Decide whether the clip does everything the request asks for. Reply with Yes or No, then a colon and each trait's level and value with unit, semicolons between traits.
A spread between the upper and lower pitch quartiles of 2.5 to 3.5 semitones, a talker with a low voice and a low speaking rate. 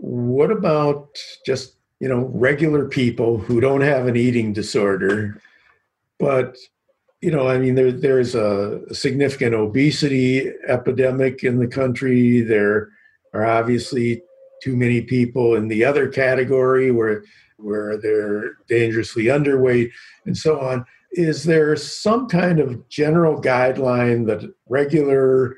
Yes: average, 3.2 semitones; low, 130 Hz; slow, 130 wpm